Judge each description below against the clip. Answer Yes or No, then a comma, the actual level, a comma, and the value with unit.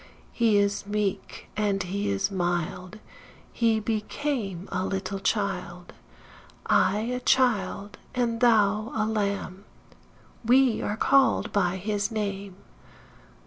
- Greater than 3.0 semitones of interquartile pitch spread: No, narrow, 2.4 semitones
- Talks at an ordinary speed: No, slow, 110 wpm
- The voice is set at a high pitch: Yes, high, 205 Hz